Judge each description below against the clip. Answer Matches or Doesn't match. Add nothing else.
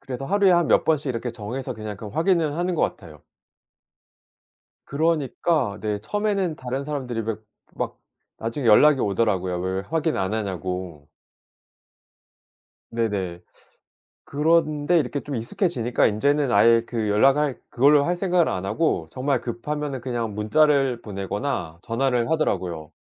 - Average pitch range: Doesn't match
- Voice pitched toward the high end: Doesn't match